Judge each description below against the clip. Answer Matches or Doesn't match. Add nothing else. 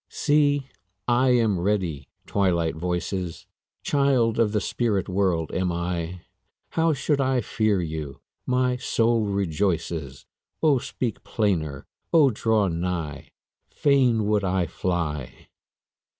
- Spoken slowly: Matches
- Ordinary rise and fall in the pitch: Doesn't match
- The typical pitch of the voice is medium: Doesn't match